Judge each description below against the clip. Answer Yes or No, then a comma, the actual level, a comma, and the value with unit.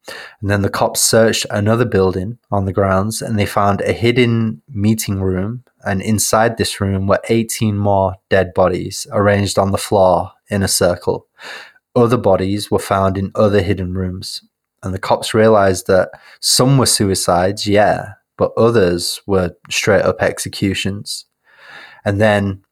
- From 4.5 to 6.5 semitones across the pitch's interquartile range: No, narrow, 2.5 semitones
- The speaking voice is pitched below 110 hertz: Yes, low, 100 Hz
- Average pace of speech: Yes, average, 155 wpm